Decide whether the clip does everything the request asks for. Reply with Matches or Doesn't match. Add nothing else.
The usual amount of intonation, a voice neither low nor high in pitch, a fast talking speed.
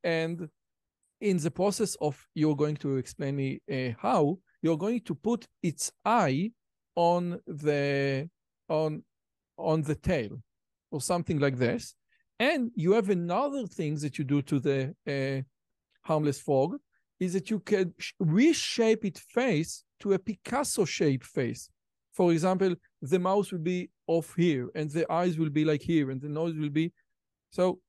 Matches